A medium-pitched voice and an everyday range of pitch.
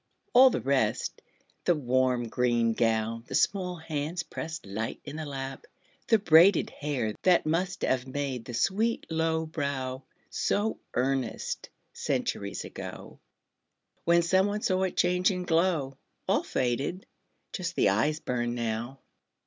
No: medium, 145 Hz; wide, 6.1 semitones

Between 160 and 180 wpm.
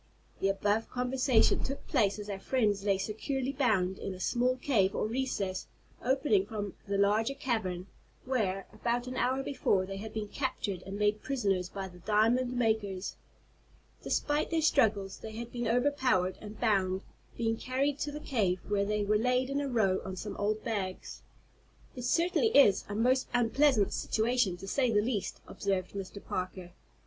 Yes: average, 170 wpm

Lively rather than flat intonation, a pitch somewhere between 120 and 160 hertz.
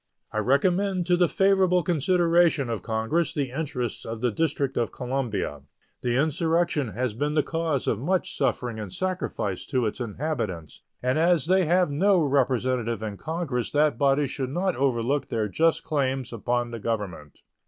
Yes: wide, 5.9 semitones; low, 135 Hz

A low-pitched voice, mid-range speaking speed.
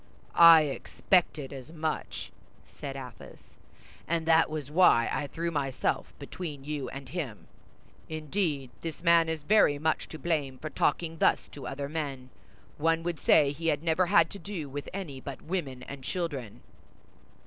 No: medium, 155 Hz; average, 160 wpm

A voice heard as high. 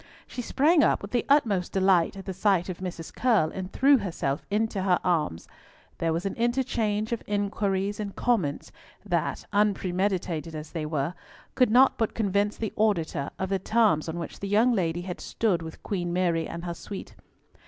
Yes: high, 195 Hz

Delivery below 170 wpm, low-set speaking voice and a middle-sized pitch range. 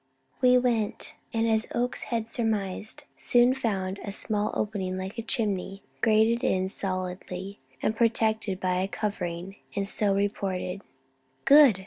No: slow, 135 wpm; high, 205 Hz; average, 3.1 semitones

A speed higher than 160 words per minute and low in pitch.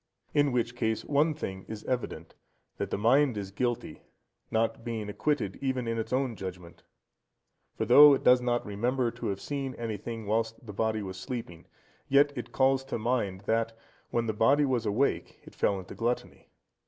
Yes: average, 180 wpm; low, 115 Hz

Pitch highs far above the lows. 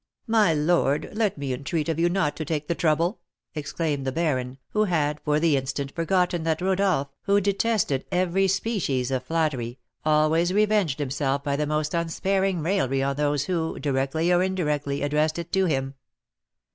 No: average, 4.2 semitones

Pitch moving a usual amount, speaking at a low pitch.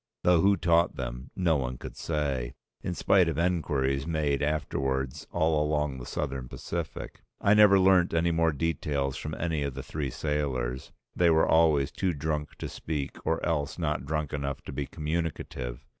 Yes: average, 3.2 semitones; very low, 75 Hz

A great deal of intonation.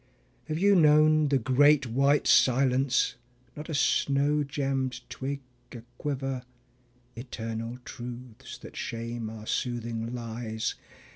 No: average, 3.4 semitones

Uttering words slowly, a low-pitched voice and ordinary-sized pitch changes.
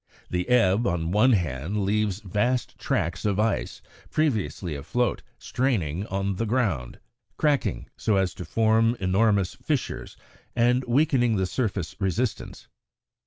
Yes: slow, 125 wpm; low, 105 Hz; average, 4.7 semitones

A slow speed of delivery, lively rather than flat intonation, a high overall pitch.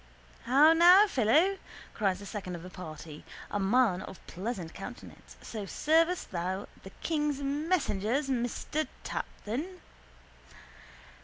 Yes: slow, 120 wpm; wide, 8.3 semitones; high, 240 Hz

